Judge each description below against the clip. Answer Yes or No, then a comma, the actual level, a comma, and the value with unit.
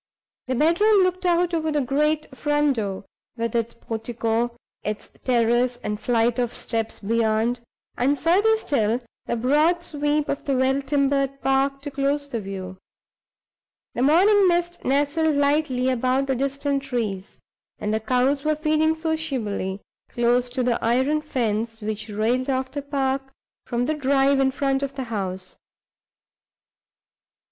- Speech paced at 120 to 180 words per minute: Yes, average, 145 wpm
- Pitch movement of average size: Yes, average, 4.0 semitones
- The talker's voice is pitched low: No, very high, 270 Hz